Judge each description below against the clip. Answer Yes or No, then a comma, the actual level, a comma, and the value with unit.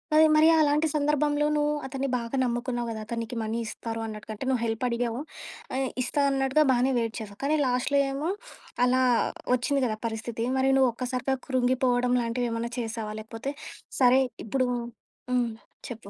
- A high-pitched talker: Yes, very high, 250 Hz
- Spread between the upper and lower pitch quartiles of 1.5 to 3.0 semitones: Yes, average, 2.7 semitones